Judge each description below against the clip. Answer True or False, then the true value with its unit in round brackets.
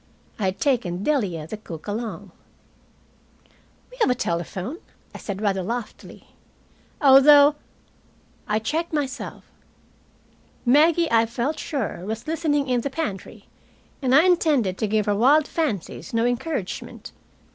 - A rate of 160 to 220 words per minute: False (135 wpm)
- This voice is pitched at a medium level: False (245 Hz)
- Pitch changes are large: True (6.1 semitones)